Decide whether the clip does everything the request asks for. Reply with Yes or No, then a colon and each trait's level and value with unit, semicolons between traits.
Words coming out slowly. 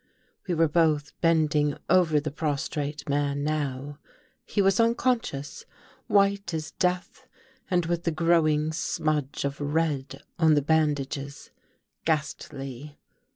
Yes: slow, 120 wpm